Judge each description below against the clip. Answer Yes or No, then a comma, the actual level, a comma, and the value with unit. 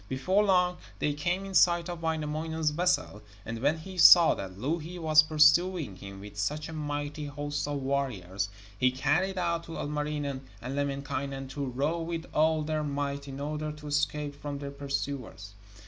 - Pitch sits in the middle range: Yes, medium, 150 Hz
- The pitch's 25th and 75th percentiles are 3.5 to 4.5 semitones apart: No, average, 2.7 semitones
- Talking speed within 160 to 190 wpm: Yes, average, 170 wpm